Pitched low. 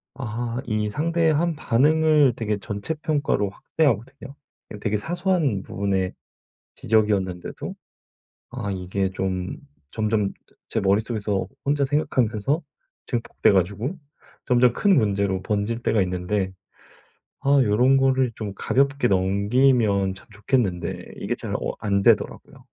Yes: low, 110 Hz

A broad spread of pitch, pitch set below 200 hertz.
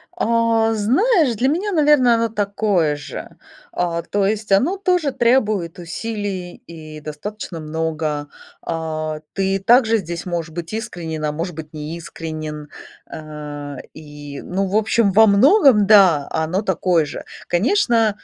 Yes: wide, 5.9 semitones; medium, 185 Hz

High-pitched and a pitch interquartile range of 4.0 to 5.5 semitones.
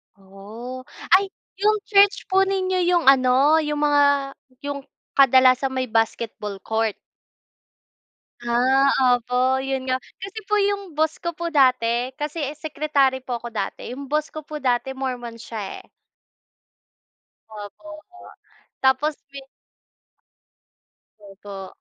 Yes: very high, 270 Hz; average, 4.3 semitones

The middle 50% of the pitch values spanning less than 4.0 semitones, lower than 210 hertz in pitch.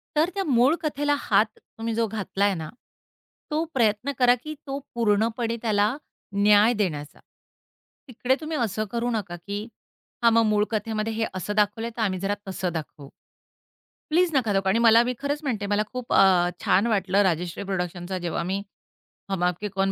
No: average, 3.6 semitones; high, 215 Hz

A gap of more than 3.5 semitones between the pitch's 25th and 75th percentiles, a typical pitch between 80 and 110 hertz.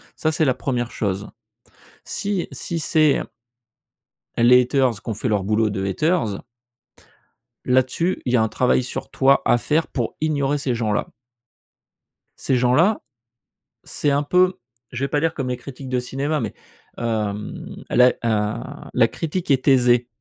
No: average, 4.0 semitones; low, 125 Hz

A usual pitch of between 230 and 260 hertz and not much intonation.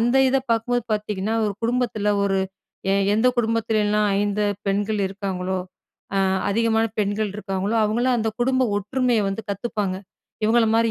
No: high, 215 Hz; narrow, 2.2 semitones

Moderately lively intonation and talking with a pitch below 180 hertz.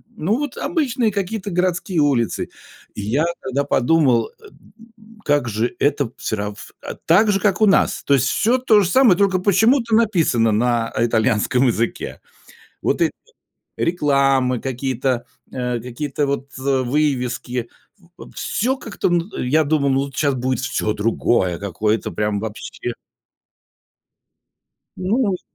No: wide, 7.8 semitones; medium, 140 Hz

